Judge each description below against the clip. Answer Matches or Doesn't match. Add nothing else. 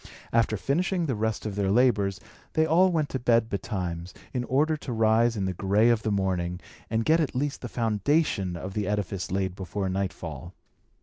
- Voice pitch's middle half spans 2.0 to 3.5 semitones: Doesn't match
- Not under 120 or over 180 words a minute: Doesn't match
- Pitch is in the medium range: Doesn't match